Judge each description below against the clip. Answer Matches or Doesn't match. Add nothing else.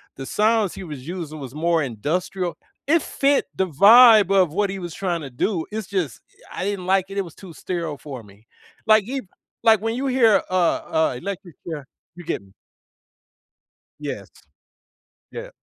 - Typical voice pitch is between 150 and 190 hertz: Matches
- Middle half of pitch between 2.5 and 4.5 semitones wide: Doesn't match